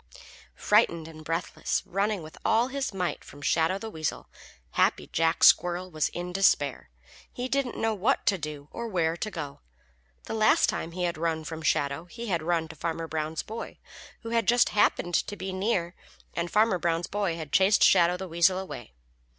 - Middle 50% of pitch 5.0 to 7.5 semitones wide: No, average, 4.2 semitones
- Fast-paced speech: No, average, 190 wpm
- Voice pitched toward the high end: No, medium, 175 Hz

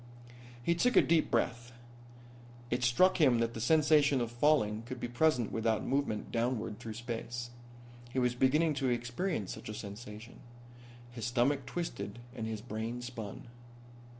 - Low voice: Yes, low, 120 Hz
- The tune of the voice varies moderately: Yes, average, 3.6 semitones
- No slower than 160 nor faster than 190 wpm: No, average, 150 wpm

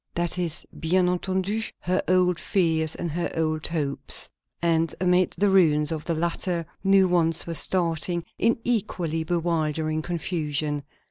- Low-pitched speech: No, medium, 170 Hz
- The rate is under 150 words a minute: Yes, average, 140 wpm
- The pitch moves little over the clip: Yes, narrow, 2.2 semitones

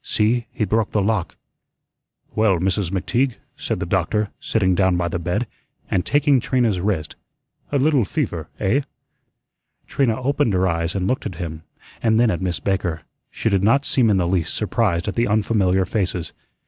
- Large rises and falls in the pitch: No, average, 4.2 semitones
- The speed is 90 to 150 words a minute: No, average, 175 wpm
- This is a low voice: Yes, low, 100 Hz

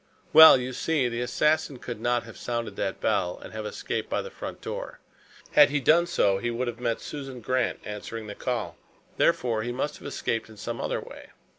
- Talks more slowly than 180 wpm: No, fast, 205 wpm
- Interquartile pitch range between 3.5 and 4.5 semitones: No, average, 2.9 semitones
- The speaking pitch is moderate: No, low, 120 Hz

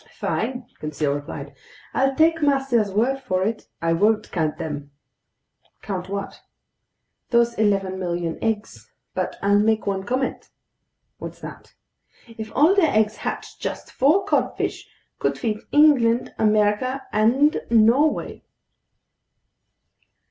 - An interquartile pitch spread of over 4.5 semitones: Yes, average, 5.3 semitones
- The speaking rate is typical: No, slow, 115 wpm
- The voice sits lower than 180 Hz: No, high, 220 Hz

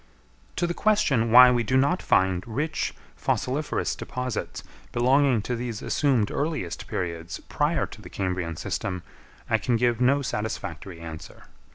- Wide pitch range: Yes, wide, 6.6 semitones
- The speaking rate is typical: Yes, average, 145 wpm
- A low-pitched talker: Yes, low, 120 Hz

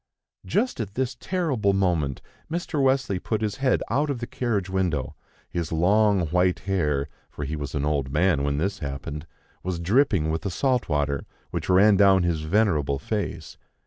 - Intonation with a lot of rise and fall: Yes, wide, 6.2 semitones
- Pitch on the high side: No, very low, 95 Hz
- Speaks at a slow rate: No, average, 175 wpm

